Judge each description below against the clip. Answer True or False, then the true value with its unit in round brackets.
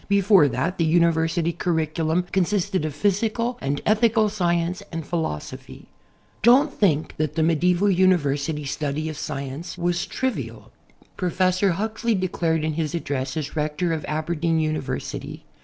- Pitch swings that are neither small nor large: True (3.5 semitones)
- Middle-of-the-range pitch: True (170 Hz)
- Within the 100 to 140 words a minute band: True (135 wpm)